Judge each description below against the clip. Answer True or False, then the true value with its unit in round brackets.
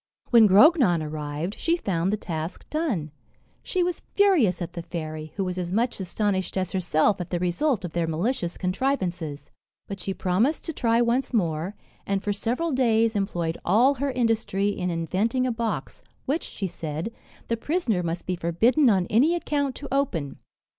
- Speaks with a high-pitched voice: True (200 Hz)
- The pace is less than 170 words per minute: False (175 wpm)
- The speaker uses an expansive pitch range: True (6.4 semitones)